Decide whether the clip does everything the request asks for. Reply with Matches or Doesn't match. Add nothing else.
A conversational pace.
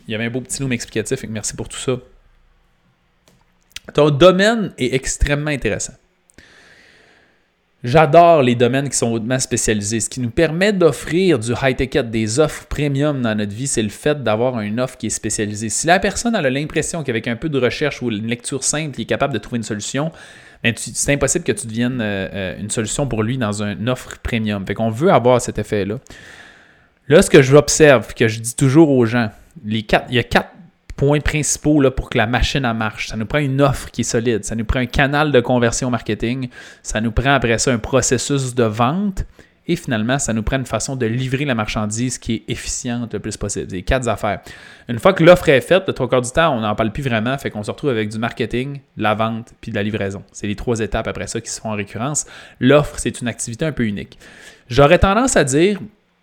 Doesn't match